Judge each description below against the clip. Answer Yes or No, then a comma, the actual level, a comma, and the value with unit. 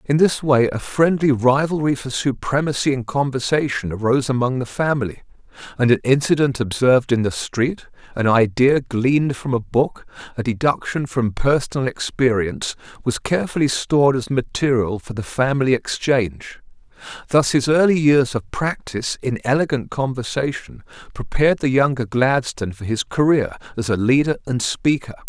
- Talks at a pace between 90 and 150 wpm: Yes, average, 145 wpm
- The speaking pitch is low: Yes, low, 130 Hz